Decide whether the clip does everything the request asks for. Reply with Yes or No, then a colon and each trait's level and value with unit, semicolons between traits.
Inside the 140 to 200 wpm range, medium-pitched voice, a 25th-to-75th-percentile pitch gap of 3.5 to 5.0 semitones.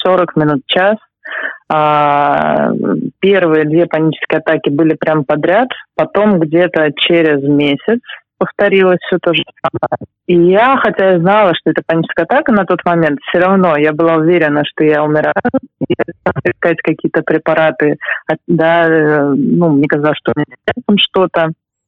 No: average, 150 wpm; medium, 165 Hz; average, 3.1 semitones